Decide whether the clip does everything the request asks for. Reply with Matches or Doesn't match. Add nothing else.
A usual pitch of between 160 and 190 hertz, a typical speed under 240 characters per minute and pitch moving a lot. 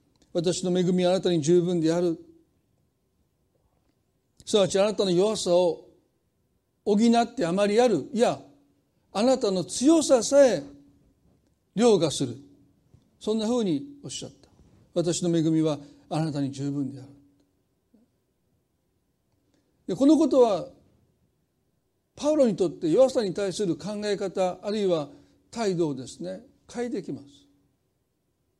Matches